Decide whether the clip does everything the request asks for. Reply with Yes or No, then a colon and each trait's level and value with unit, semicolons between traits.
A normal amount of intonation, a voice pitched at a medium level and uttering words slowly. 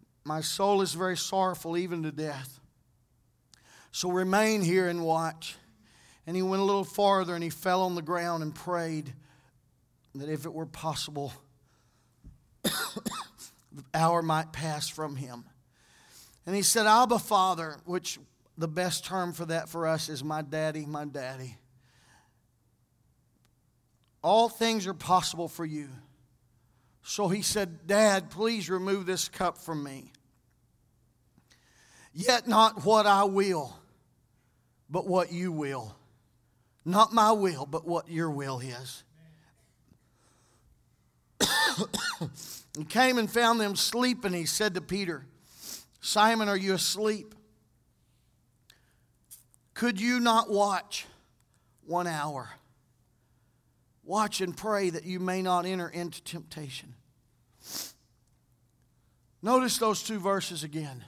No: wide, 6.3 semitones; medium, 165 Hz; slow, 120 wpm